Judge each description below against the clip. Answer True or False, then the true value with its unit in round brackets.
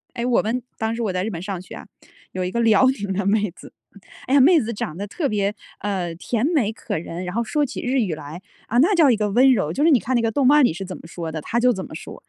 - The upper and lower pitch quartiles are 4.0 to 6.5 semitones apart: True (5.2 semitones)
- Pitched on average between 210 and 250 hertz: True (220 Hz)